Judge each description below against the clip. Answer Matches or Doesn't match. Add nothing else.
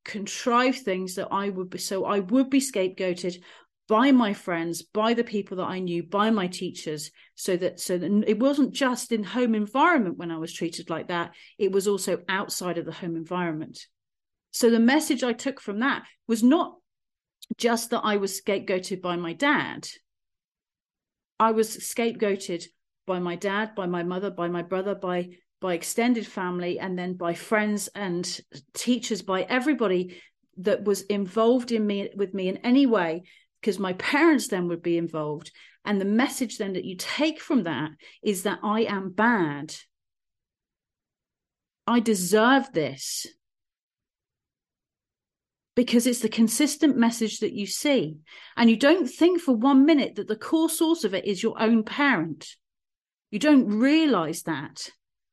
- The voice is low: Doesn't match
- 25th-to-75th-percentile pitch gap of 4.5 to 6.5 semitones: Matches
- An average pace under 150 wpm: Doesn't match